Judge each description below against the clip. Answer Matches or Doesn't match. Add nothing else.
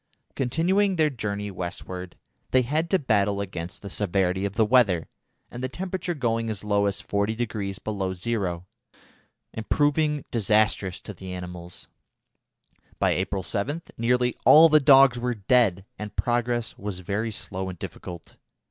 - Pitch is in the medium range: Doesn't match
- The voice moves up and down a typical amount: Matches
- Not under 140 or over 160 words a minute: Matches